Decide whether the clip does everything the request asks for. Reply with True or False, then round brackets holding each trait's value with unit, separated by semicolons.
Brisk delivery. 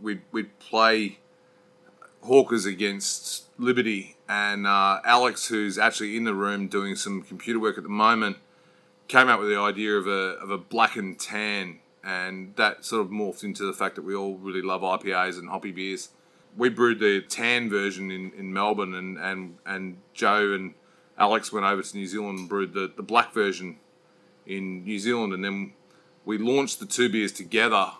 False (185 wpm)